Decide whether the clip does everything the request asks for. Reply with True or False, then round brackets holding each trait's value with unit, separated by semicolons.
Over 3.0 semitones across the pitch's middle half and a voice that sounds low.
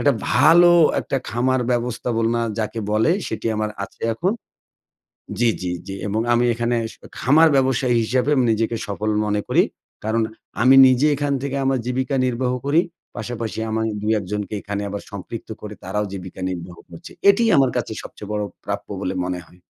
True (3.8 semitones; 115 Hz)